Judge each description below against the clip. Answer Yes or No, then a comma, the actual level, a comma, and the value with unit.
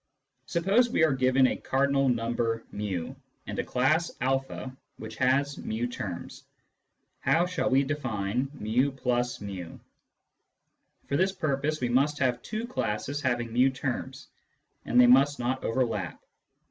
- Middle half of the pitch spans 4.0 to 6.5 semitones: No, average, 3.0 semitones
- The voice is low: Yes, low, 130 Hz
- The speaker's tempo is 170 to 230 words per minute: No, slow, 135 wpm